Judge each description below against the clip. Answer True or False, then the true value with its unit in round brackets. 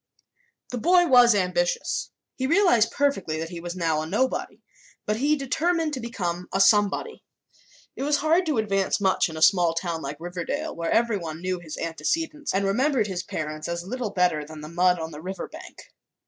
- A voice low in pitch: False (195 Hz)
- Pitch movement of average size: False (7.5 semitones)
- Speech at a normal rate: True (190 wpm)